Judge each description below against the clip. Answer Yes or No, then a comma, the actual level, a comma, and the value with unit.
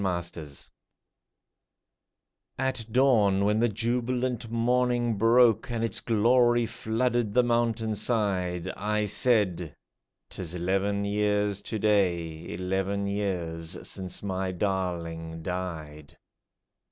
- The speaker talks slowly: Yes, slow, 105 wpm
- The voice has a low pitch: Yes, low, 100 Hz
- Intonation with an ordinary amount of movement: Yes, average, 4.2 semitones